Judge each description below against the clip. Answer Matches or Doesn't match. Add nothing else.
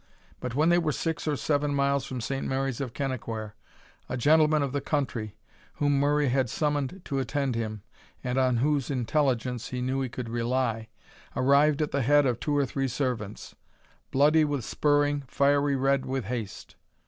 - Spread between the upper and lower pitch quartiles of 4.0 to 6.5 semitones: Doesn't match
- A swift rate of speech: Doesn't match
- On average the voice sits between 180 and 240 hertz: Doesn't match